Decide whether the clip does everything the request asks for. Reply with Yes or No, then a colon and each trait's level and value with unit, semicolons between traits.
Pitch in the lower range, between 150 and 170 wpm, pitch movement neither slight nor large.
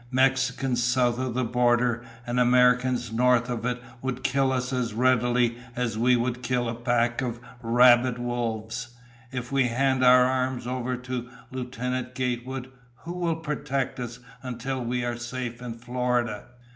No: low, 125 Hz; average, 155 wpm; narrow, 1.1 semitones